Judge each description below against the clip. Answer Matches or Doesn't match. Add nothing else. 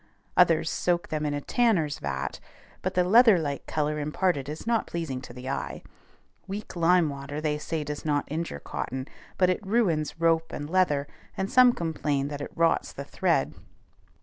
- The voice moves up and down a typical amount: Matches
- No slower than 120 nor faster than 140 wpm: Doesn't match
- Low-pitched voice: Doesn't match